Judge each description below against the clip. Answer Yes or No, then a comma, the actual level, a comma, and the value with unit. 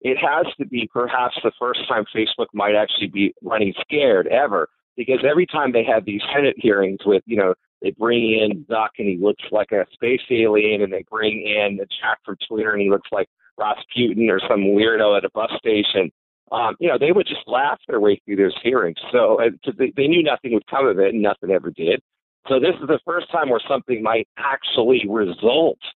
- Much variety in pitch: No, average, 4.2 semitones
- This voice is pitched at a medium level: No, low, 110 Hz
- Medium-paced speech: No, fast, 215 wpm